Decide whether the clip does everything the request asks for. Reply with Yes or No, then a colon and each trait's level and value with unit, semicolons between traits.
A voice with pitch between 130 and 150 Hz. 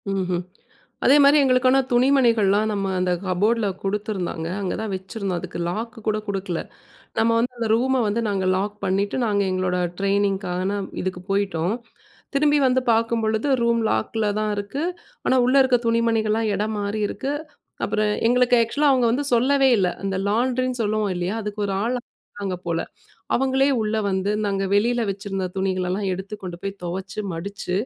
No: high, 210 Hz